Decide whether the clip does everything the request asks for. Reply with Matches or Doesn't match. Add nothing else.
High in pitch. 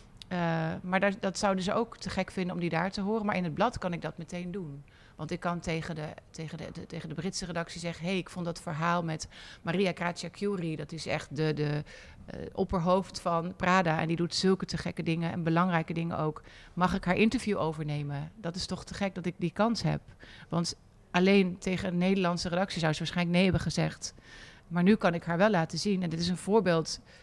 Doesn't match